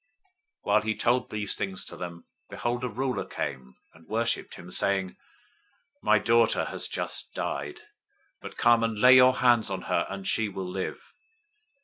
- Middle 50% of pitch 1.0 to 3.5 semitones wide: No, average, 4.0 semitones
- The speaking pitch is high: No, low, 105 Hz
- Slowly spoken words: No, average, 165 wpm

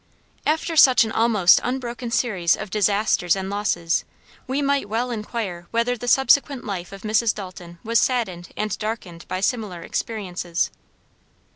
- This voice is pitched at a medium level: No, high, 215 Hz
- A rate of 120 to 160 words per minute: Yes, average, 145 wpm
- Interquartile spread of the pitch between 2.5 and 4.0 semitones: No, average, 4.6 semitones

